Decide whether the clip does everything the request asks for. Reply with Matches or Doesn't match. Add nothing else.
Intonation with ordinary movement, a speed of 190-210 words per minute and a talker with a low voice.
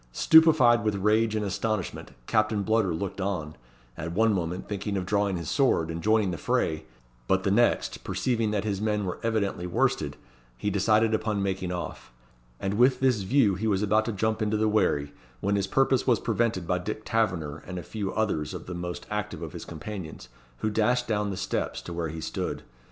Matches